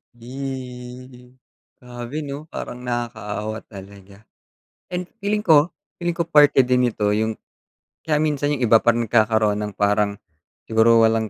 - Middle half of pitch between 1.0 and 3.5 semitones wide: No, average, 4.4 semitones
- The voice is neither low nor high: No, low, 120 Hz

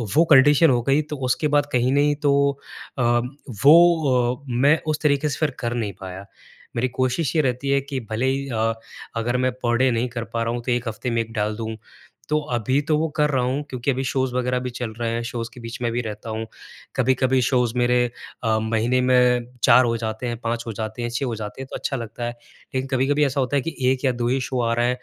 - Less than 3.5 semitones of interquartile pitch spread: Yes, narrow, 2.5 semitones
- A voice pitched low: Yes, low, 125 Hz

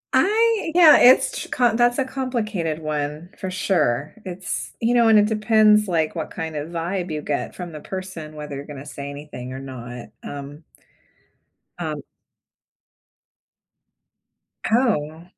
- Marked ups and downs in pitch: Yes, wide, 6.8 semitones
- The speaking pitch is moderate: Yes, medium, 175 Hz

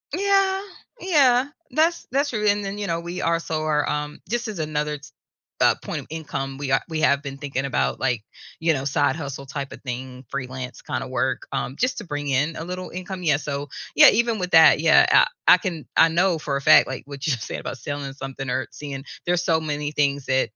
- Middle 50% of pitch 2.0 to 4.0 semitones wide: No, average, 4.8 semitones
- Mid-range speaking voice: Yes, medium, 150 Hz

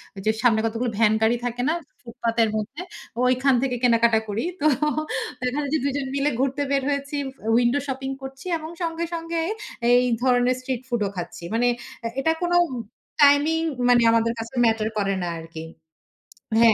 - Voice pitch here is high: Yes, high, 245 Hz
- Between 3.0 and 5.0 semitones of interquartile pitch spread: Yes, average, 3.6 semitones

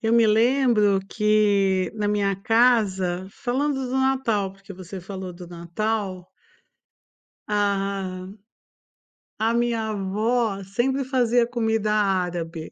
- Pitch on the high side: Yes, high, 210 Hz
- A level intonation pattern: No, average, 3.5 semitones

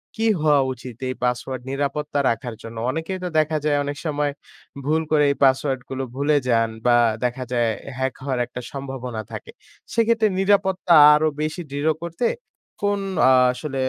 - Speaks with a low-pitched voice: No, medium, 145 Hz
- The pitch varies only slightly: No, average, 3.5 semitones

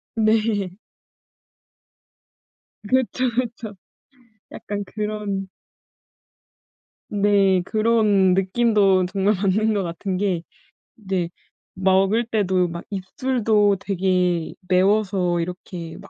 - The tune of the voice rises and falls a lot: No, narrow, 2.5 semitones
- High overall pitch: Yes, high, 195 Hz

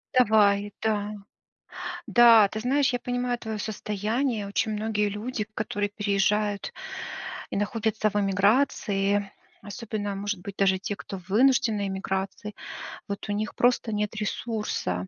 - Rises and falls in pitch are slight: Yes, narrow, 1.7 semitones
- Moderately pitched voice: No, high, 210 Hz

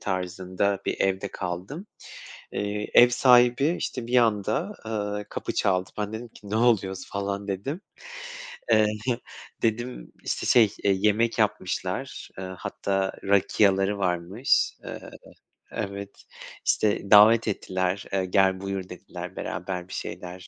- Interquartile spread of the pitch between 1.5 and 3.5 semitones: Yes, average, 2.8 semitones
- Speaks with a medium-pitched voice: No, low, 100 Hz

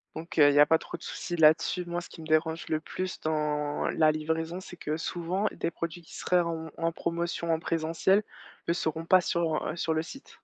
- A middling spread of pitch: No, narrow, 1.6 semitones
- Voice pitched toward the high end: No, medium, 165 Hz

